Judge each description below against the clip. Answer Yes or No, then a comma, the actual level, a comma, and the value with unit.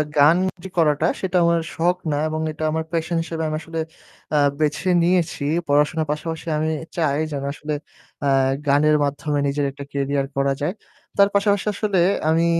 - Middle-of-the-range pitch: Yes, medium, 155 Hz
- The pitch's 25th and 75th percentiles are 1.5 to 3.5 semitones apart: Yes, average, 2.7 semitones